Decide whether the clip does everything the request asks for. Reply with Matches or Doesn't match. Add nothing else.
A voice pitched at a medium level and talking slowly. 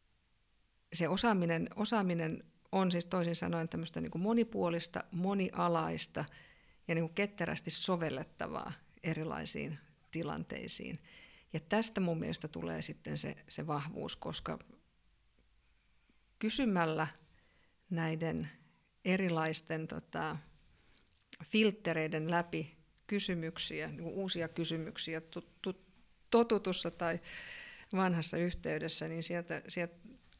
Matches